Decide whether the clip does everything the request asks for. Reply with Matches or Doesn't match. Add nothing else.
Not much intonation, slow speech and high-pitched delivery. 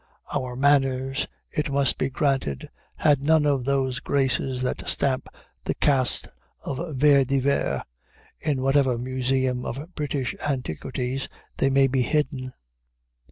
Doesn't match